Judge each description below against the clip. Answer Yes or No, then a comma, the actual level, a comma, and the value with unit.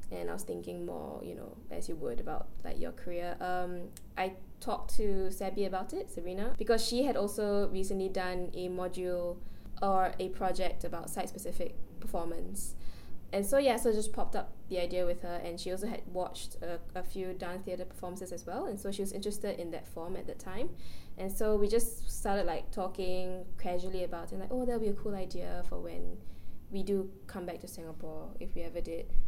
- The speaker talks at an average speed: No, fast, 210 wpm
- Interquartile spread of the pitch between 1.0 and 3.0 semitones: Yes, narrow, 2.4 semitones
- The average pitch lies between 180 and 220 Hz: Yes, medium, 185 Hz